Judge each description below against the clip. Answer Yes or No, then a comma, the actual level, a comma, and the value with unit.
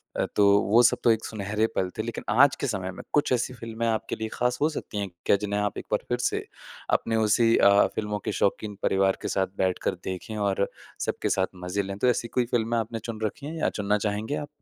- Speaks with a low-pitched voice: Yes, low, 110 Hz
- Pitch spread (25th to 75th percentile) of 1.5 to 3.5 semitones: Yes, narrow, 2.6 semitones